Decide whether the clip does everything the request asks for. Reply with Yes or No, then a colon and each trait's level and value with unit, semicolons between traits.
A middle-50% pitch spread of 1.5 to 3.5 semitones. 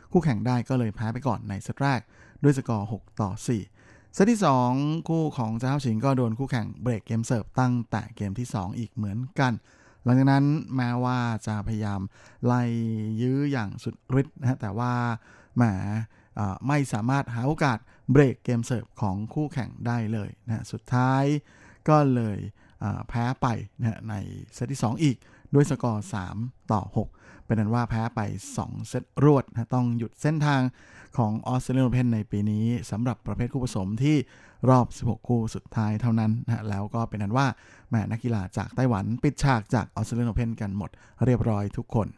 Yes: average, 2.8 semitones